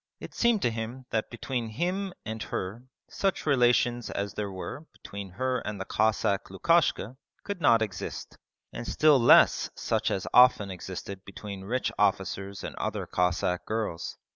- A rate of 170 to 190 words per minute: No, average, 155 wpm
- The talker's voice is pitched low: Yes, low, 110 Hz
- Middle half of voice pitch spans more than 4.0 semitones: Yes, average, 4.6 semitones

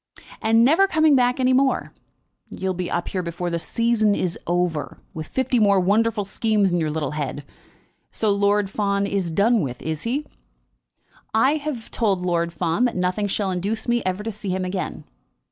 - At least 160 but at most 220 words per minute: Yes, average, 180 wpm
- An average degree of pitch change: Yes, average, 4.4 semitones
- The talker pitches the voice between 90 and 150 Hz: No, high, 200 Hz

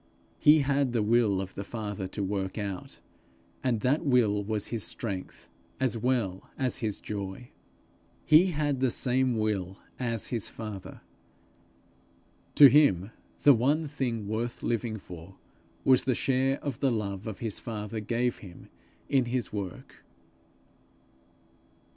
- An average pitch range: Yes, average, 4.3 semitones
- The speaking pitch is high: No, low, 115 Hz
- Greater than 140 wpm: No, slow, 135 wpm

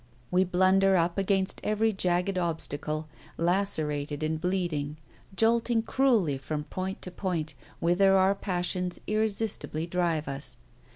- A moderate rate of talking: No, slow, 120 wpm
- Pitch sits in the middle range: Yes, medium, 180 Hz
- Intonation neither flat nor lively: Yes, average, 3.8 semitones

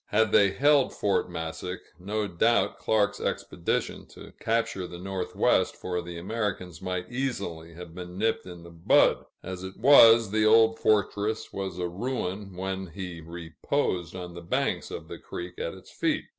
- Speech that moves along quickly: No, average, 165 wpm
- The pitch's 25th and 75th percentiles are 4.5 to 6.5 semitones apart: No, average, 3.7 semitones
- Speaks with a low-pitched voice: Yes, very low, 95 Hz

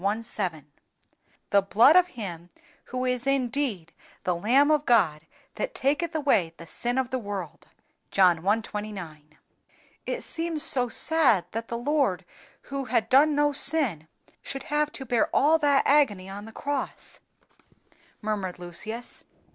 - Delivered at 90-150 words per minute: Yes, average, 145 wpm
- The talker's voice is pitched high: Yes, high, 240 Hz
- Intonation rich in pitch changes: Yes, wide, 6.8 semitones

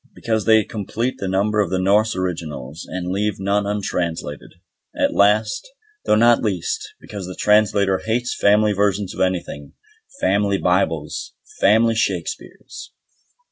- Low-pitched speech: Yes, low, 100 Hz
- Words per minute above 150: No, slow, 135 wpm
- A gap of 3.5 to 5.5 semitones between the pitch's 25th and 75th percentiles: No, narrow, 2.5 semitones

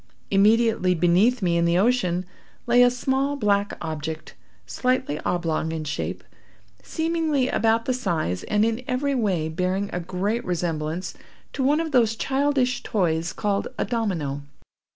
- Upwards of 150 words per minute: No, average, 145 wpm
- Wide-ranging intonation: Yes, wide, 6.6 semitones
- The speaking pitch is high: Yes, high, 205 Hz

